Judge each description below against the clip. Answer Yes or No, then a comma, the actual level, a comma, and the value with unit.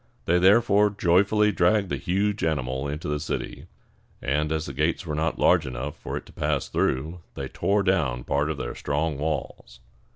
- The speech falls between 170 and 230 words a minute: Yes, average, 185 wpm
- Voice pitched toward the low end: Yes, very low, 80 Hz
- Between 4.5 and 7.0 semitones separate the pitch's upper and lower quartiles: Yes, average, 4.9 semitones